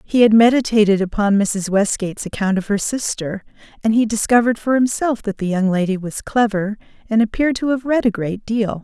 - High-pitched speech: Yes, high, 215 Hz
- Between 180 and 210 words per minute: Yes, average, 195 wpm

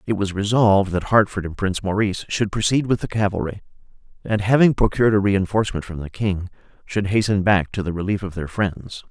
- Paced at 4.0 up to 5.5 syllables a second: No, 5.9 syllables/s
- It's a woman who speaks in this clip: No, male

